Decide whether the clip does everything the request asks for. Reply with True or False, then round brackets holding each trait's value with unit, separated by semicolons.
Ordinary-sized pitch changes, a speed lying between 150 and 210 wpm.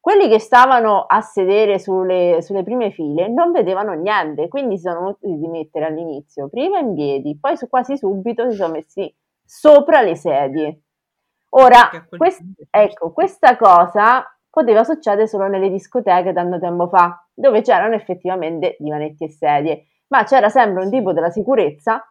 False (6.5 semitones; 155 wpm)